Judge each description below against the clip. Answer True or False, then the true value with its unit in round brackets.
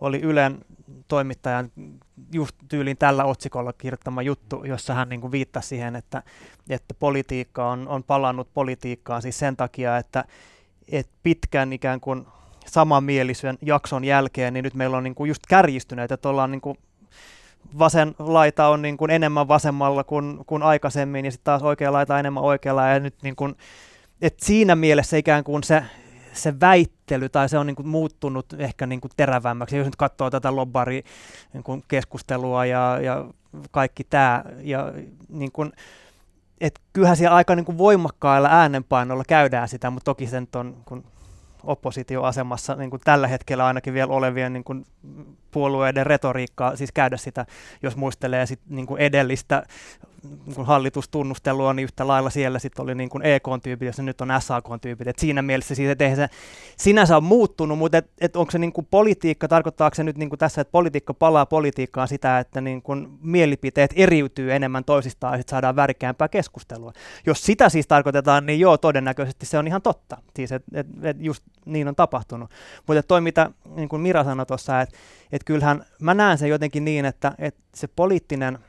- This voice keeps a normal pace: False (160 wpm)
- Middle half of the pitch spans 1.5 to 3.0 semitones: True (2.7 semitones)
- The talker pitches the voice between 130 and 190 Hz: True (135 Hz)